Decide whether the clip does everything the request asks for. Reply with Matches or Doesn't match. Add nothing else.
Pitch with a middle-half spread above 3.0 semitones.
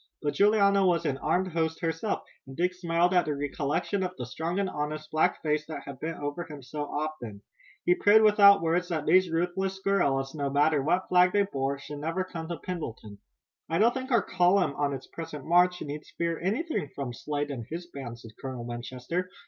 Matches